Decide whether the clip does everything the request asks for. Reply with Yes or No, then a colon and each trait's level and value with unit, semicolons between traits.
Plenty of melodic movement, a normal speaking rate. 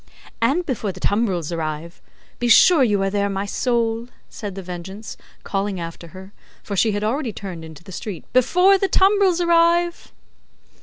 Yes: wide, 6.2 semitones; average, 165 wpm